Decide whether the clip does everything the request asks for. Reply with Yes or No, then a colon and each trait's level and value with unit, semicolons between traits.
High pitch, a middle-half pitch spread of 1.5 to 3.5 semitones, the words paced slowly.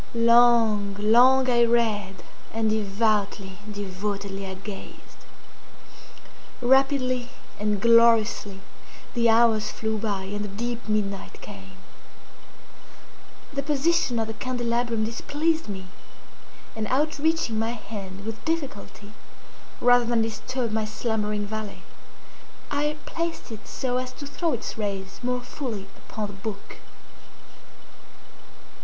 Yes: high, 225 Hz; average, 3.1 semitones; slow, 110 wpm